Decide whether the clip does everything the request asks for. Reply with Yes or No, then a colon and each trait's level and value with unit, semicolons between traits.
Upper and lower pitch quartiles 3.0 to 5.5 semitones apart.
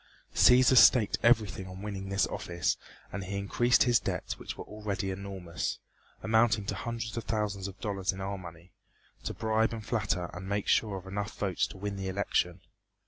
No: narrow, 2.5 semitones